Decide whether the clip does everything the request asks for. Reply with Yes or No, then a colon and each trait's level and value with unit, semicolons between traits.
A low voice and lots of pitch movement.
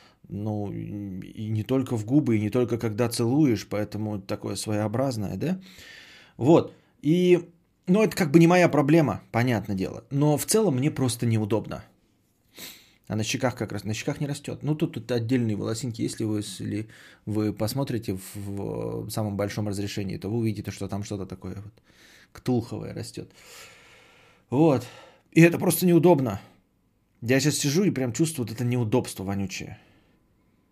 Yes: low, 115 Hz; wide, 5.9 semitones